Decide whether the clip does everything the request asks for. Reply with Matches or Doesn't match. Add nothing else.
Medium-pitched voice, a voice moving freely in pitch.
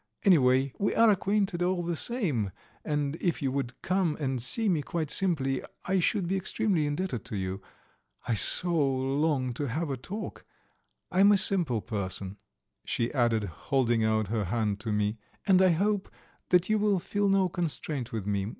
Matches